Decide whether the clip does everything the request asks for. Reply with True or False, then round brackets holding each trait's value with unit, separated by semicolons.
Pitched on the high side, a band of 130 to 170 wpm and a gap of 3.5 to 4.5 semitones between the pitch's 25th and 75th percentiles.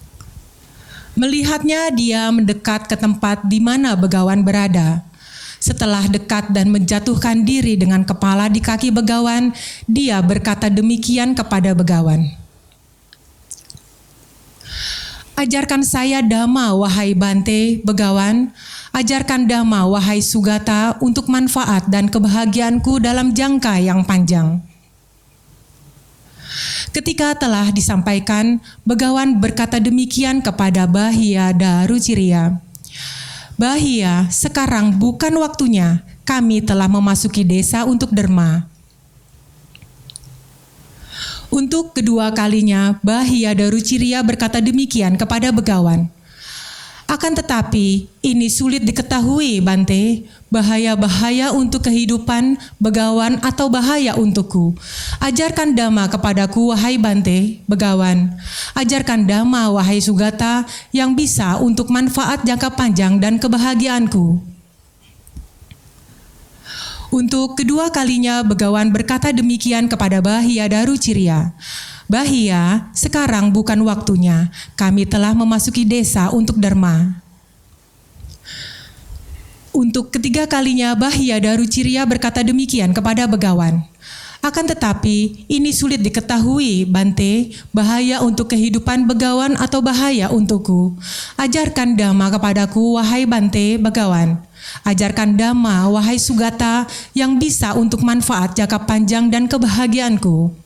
False (220 Hz; 95 wpm; 3.9 semitones)